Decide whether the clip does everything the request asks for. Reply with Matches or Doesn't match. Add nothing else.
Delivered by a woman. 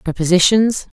Matches